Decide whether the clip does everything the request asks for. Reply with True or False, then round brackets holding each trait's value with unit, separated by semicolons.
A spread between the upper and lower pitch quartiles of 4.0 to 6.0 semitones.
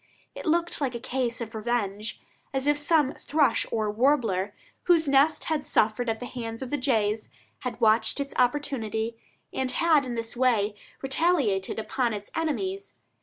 True (4.7 semitones)